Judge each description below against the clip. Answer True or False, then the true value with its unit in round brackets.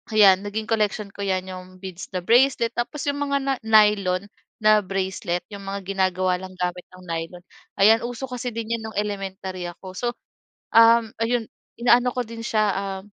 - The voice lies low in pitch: False (200 Hz)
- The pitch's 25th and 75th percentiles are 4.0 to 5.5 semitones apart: False (3.5 semitones)